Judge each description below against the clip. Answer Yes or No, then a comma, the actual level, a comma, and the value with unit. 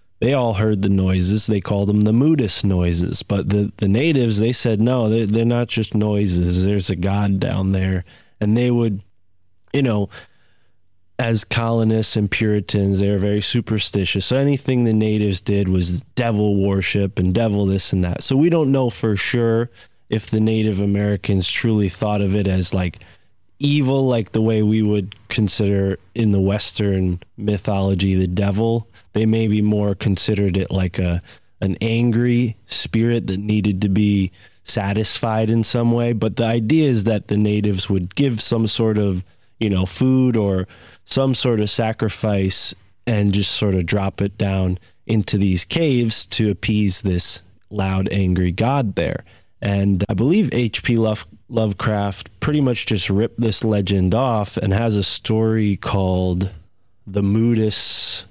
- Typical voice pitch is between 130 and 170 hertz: No, low, 105 Hz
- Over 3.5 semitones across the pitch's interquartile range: No, average, 2.8 semitones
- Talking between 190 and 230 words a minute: No, average, 165 wpm